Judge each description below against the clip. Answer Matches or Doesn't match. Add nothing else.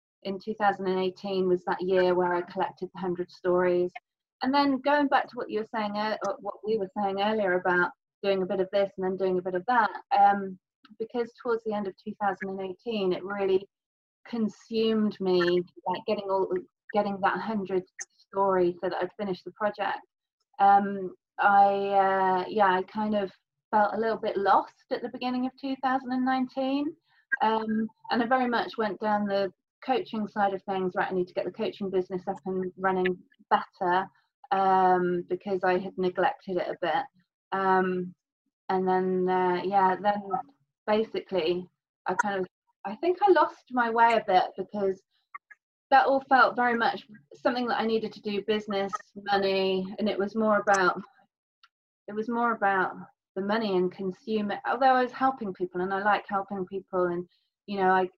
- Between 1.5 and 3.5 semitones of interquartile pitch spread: Matches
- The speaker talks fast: Doesn't match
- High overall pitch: Matches